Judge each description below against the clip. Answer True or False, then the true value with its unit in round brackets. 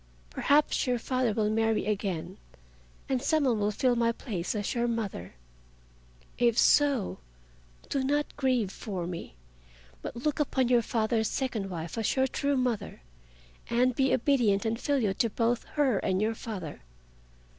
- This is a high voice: True (230 Hz)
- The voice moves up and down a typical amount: True (4.0 semitones)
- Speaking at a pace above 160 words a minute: False (155 wpm)